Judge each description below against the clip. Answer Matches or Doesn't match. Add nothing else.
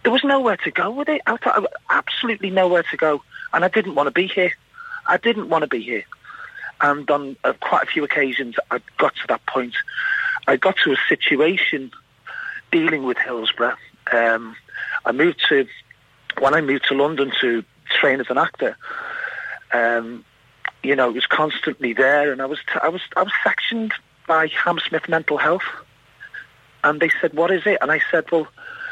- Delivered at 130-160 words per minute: Doesn't match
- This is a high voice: Matches